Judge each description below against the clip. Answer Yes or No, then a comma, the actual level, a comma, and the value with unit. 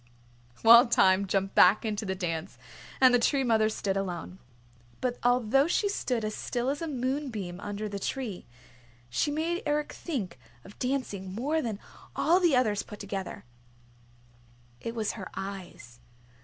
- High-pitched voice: Yes, high, 220 Hz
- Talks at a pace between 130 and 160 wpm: Yes, average, 155 wpm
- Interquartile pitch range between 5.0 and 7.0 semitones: Yes, average, 5.3 semitones